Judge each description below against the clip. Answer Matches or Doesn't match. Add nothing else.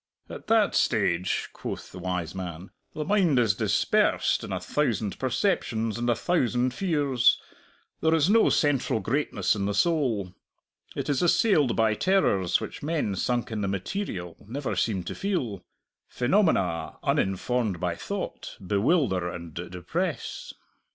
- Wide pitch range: Matches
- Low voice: Matches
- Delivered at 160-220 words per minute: Doesn't match